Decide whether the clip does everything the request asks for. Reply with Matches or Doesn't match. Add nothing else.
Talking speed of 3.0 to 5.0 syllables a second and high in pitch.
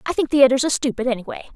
Doesn't match